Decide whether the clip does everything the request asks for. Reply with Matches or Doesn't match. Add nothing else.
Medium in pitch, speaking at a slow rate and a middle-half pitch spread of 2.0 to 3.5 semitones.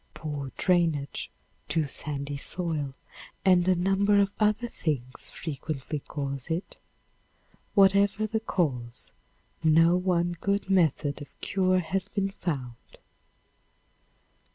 Doesn't match